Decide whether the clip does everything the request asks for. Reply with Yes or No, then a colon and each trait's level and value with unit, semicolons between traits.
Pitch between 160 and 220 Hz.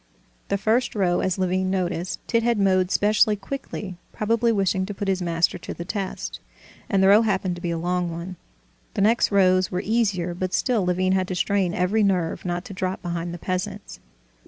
Yes: high, 190 Hz